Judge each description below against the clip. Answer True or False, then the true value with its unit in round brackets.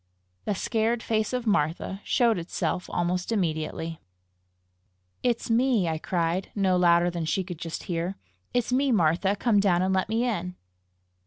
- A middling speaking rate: True (155 wpm)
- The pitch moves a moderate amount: True (4.6 semitones)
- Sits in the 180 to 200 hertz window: True (190 Hz)